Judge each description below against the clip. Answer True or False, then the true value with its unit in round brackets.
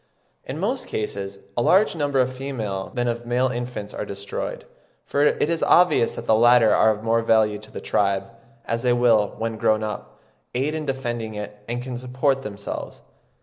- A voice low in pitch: True (120 Hz)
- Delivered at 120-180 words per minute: False (190 wpm)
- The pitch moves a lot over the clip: False (3.5 semitones)